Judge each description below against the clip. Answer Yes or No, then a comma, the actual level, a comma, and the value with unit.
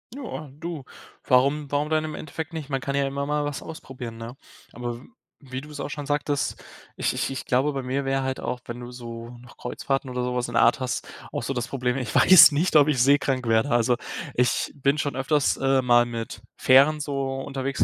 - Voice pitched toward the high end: No, low, 135 Hz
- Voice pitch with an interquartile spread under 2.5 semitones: No, average, 2.8 semitones